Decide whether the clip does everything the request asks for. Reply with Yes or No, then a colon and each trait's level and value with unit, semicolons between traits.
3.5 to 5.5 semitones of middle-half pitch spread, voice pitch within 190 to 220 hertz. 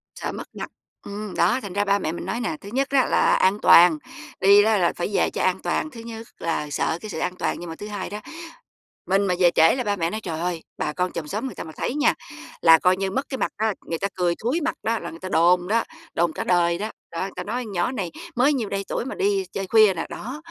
Yes: average, 4.7 semitones; high, 200 Hz